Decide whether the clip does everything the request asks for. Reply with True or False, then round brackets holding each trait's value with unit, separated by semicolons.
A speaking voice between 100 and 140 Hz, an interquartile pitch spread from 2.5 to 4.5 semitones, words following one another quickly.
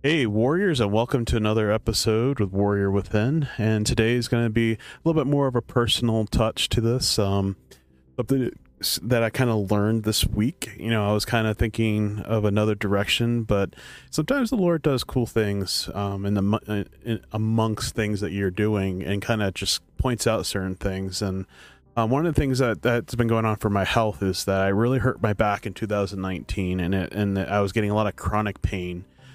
True (110 Hz; 2.9 semitones; 210 wpm)